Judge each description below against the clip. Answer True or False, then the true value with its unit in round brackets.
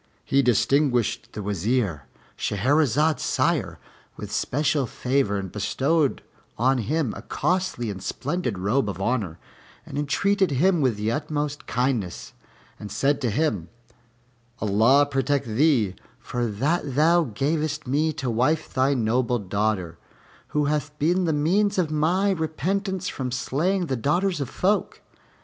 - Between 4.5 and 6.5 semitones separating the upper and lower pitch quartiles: True (5.5 semitones)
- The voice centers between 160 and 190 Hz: False (140 Hz)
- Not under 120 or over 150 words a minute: True (135 wpm)